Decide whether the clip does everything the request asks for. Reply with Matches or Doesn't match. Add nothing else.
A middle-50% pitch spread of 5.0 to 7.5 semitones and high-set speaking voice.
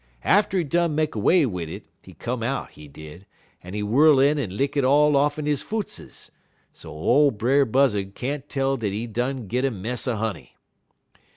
Doesn't match